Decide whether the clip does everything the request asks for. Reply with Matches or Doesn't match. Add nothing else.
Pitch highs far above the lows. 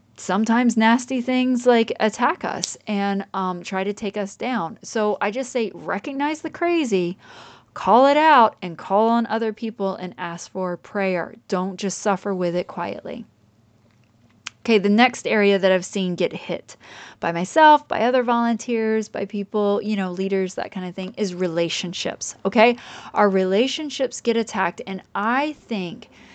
Doesn't match